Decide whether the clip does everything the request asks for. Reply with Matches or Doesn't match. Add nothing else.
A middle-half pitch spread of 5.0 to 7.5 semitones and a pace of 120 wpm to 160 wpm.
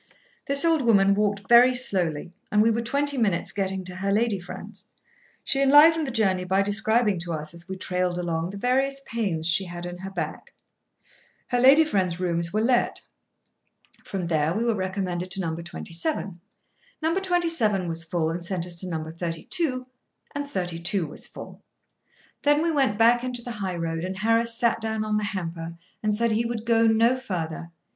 Doesn't match